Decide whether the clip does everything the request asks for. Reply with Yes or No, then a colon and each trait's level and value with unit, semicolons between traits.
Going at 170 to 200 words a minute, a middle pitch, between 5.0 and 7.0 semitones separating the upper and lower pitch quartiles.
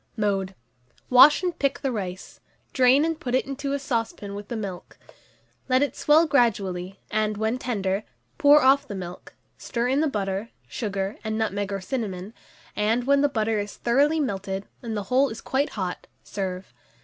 No: average, 175 wpm; high, 220 Hz; average, 5.3 semitones